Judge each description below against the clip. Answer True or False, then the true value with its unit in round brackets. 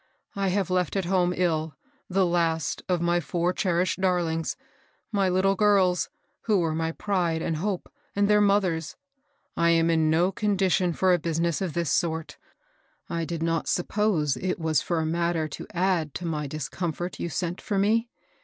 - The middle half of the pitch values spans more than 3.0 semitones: False (2.6 semitones)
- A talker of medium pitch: True (175 Hz)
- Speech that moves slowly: False (185 wpm)